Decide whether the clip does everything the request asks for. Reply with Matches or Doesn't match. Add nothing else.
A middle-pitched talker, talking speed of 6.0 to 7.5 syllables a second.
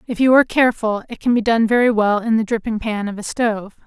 Doesn't match